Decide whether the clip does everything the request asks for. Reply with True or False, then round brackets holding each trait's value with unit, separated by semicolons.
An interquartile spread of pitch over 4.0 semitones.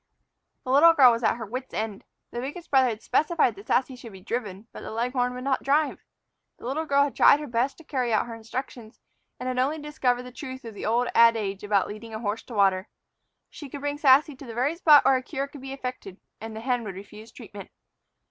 False (3.6 semitones)